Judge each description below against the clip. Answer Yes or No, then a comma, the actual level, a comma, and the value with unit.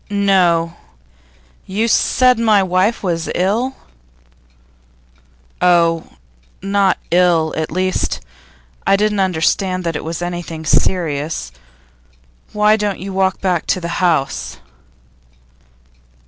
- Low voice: No, medium, 185 Hz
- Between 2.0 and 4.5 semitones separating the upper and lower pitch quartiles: Yes, average, 3.0 semitones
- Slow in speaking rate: Yes, slow, 105 wpm